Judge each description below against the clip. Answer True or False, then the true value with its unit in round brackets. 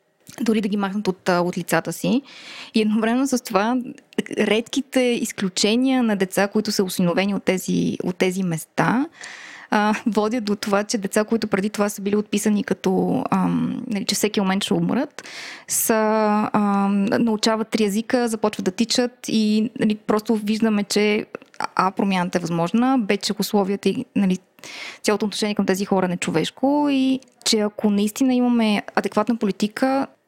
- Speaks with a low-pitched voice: False (215 Hz)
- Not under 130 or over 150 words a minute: False (160 wpm)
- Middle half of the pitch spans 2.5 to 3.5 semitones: True (2.9 semitones)